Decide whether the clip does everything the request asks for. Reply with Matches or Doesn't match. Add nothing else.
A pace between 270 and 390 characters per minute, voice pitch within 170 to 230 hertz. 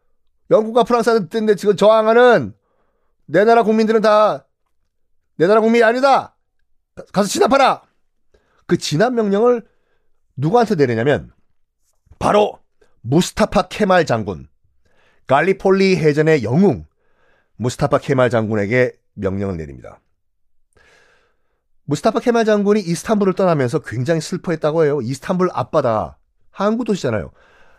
Matches